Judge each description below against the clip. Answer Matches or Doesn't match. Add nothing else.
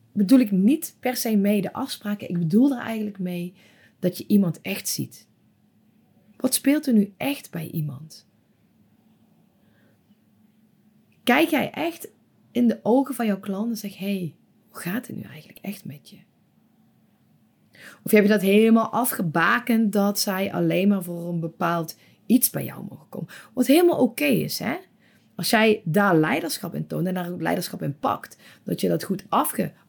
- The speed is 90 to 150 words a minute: Doesn't match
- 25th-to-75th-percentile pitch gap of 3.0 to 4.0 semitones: Doesn't match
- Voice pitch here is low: Doesn't match